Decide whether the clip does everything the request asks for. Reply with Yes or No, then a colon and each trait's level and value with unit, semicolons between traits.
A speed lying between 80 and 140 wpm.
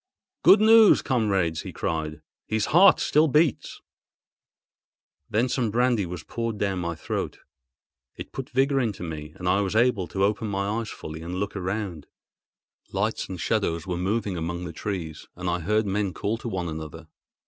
No: average, 170 wpm